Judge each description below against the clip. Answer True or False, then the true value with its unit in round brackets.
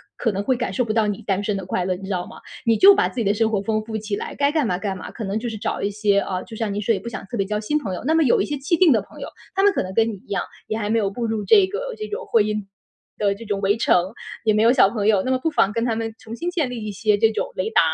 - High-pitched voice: True (220 Hz)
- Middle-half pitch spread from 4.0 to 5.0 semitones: False (3.6 semitones)